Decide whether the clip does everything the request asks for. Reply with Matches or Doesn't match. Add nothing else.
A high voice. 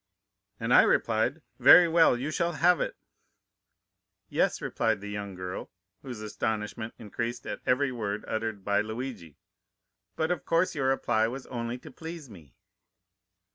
Doesn't match